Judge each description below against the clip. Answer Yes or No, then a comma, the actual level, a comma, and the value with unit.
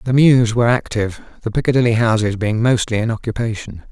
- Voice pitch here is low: Yes, low, 115 Hz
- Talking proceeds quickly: No, average, 170 wpm